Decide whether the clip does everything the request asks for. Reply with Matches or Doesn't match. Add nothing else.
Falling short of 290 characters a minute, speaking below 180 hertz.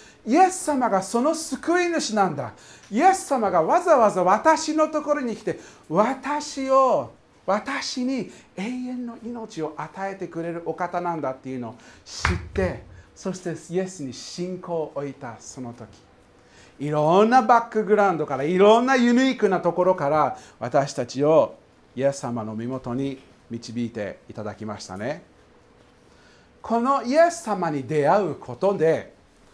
Doesn't match